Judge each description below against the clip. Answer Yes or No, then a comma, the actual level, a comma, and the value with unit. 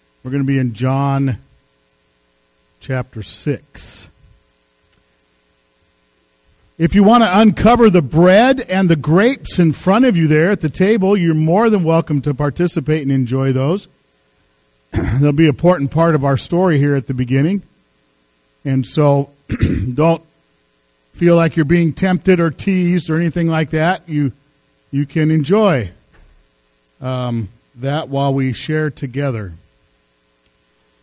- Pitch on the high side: No, medium, 140 Hz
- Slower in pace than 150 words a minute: Yes, slow, 135 wpm